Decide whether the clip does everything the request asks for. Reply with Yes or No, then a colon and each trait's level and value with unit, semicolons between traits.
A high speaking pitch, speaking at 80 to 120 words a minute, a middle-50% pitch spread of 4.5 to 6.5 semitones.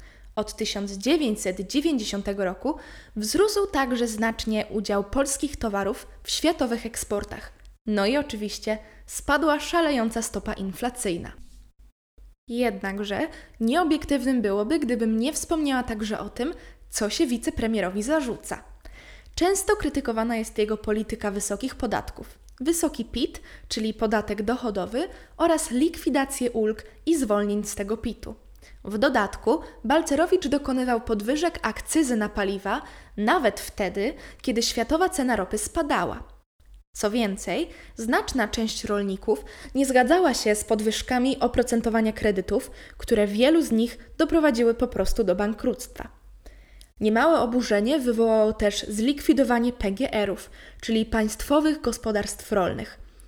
Yes: high, 235 Hz; slow, 110 wpm; average, 5.0 semitones